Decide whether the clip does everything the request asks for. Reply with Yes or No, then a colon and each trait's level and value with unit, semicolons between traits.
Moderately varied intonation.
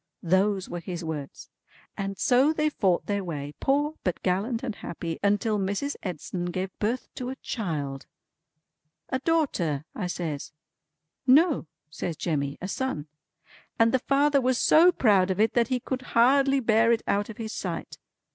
No: wide, 6.8 semitones